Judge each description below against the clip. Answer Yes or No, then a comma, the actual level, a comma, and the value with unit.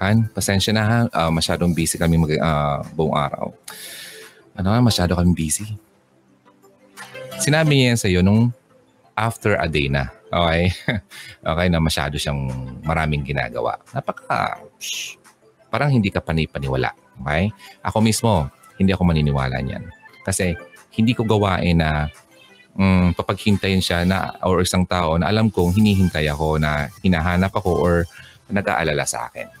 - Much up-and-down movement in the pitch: No, average, 4.9 semitones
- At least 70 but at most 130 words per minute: No, average, 145 wpm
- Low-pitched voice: Yes, very low, 90 Hz